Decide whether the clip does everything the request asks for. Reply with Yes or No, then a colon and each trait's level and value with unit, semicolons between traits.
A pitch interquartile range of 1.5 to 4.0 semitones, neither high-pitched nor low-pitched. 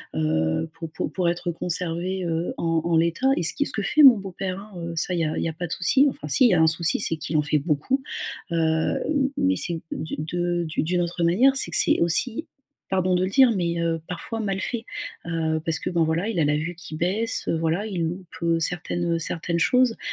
Yes: average, 2.8 semitones; medium, 170 Hz